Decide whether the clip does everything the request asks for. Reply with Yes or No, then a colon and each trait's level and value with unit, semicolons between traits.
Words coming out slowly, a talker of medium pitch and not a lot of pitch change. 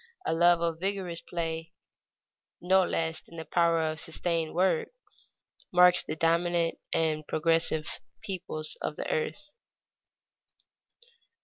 Yes: slow, 115 wpm; medium, 165 Hz; narrow, 1.5 semitones